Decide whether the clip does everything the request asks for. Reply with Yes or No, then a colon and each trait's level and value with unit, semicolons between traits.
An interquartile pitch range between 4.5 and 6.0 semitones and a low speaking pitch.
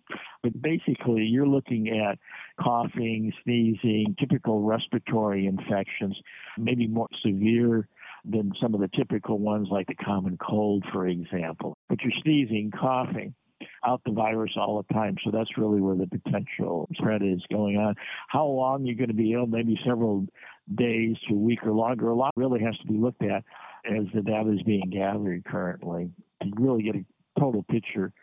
No: average, 2.7 semitones; low, 110 Hz